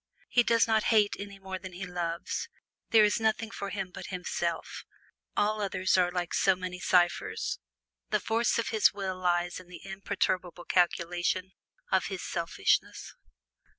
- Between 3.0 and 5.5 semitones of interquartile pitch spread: No, narrow, 2.6 semitones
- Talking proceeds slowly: No, average, 155 wpm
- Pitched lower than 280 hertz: Yes, medium, 185 Hz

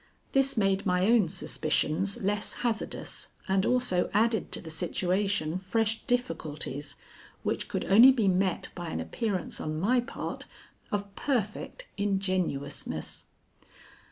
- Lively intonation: No, average, 4.0 semitones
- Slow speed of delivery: Yes, slow, 125 wpm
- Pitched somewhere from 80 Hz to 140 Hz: No, high, 195 Hz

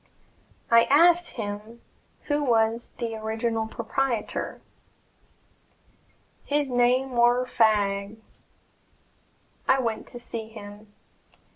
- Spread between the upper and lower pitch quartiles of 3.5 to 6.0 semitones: No, narrow, 2.5 semitones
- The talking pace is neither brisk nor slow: No, slow, 90 wpm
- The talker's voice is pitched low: No, high, 230 Hz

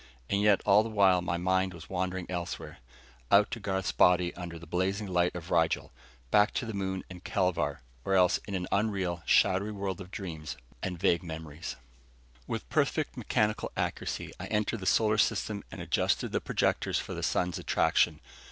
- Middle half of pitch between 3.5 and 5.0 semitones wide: No, narrow, 2.4 semitones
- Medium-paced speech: Yes, average, 180 wpm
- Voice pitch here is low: Yes, very low, 95 Hz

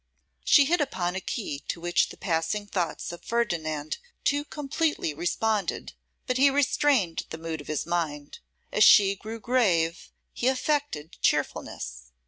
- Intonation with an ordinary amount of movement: No, wide, 7.9 semitones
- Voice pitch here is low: No, high, 190 Hz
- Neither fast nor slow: Yes, average, 145 wpm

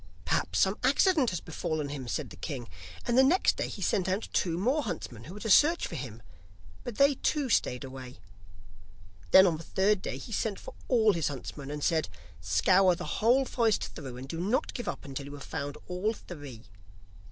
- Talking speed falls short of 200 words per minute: No, fast, 205 wpm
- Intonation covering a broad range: Yes, wide, 8.3 semitones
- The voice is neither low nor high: Yes, medium, 180 Hz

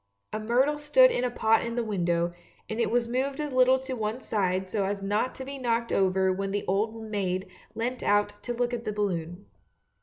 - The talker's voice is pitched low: No, high, 220 Hz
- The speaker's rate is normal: No, fast, 215 wpm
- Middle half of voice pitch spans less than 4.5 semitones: Yes, average, 4.1 semitones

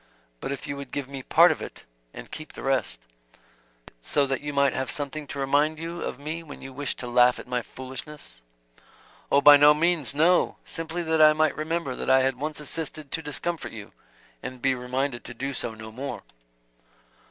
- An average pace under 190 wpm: No, fast, 205 wpm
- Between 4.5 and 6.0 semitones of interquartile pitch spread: No, average, 3.1 semitones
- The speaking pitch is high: No, medium, 140 Hz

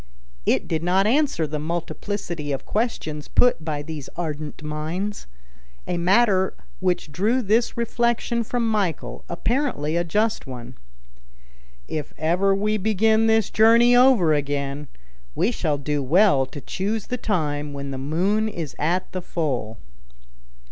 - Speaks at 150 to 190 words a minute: No, average, 140 wpm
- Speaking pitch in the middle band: Yes, medium, 175 Hz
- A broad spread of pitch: Yes, wide, 6.5 semitones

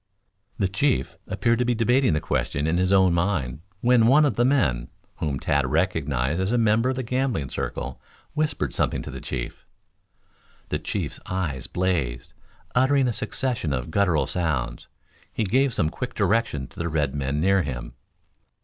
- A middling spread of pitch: No, wide, 8.7 semitones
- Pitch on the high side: No, very low, 95 Hz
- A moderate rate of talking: Yes, average, 170 wpm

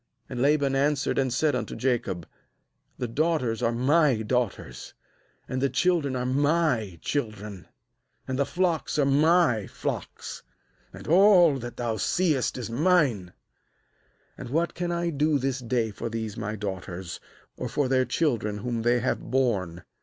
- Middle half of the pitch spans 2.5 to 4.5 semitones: No, average, 5.0 semitones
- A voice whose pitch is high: No, low, 130 Hz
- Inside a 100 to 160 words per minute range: Yes, average, 155 wpm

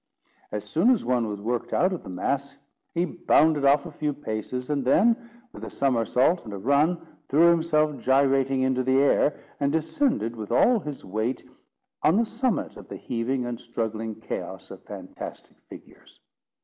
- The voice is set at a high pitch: No, medium, 140 Hz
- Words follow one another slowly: No, average, 175 wpm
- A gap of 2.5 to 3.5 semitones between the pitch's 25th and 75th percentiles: No, average, 5.3 semitones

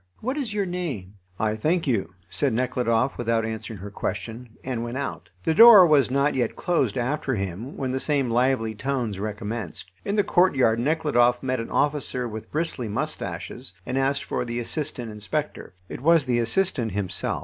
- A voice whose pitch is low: Yes, low, 125 Hz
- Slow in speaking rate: No, average, 175 wpm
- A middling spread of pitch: Yes, average, 4.8 semitones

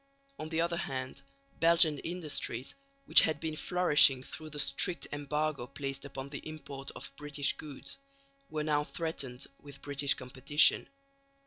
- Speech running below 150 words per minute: Yes, average, 140 wpm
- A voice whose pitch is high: No, medium, 145 Hz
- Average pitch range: No, narrow, 2.2 semitones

